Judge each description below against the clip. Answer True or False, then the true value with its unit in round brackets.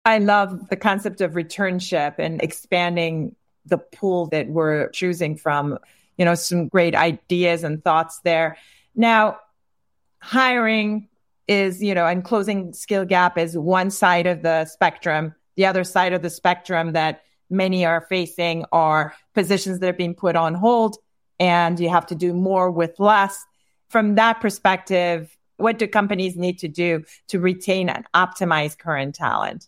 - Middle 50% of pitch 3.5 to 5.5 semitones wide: False (2.9 semitones)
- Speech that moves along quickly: False (160 wpm)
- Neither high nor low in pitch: True (180 Hz)